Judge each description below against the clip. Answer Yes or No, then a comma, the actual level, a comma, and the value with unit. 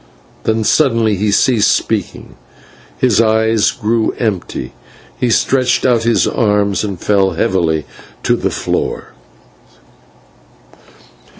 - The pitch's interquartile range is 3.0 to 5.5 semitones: No, narrow, 2.4 semitones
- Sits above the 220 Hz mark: No, low, 110 Hz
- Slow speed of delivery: Yes, slow, 105 wpm